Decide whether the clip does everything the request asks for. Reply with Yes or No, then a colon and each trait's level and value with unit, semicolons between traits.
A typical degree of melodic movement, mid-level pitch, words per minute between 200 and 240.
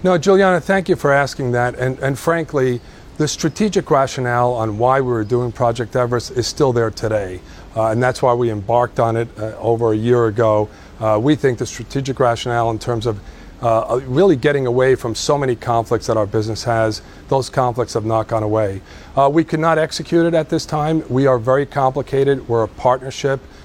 No: average, 3.6 semitones; low, 125 Hz; fast, 205 wpm